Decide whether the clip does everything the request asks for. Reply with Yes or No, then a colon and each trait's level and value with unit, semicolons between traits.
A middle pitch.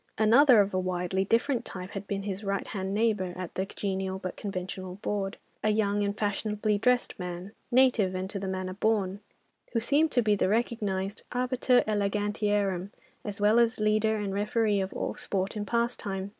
No: high, 205 Hz